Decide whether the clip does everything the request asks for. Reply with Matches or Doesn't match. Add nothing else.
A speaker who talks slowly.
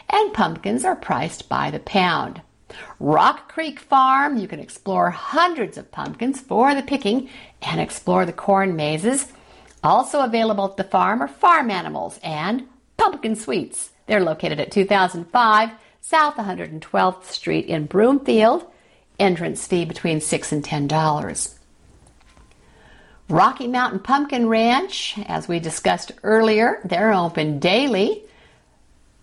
Matches